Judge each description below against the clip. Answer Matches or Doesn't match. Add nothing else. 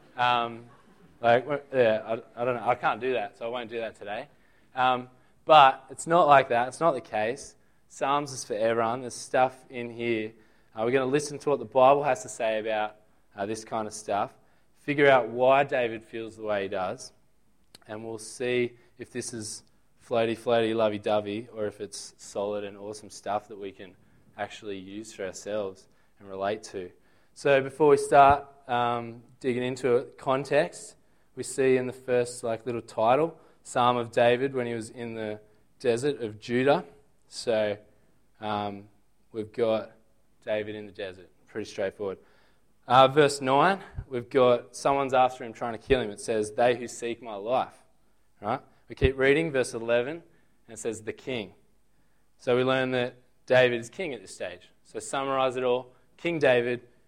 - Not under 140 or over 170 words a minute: Doesn't match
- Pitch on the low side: Matches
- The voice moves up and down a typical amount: Matches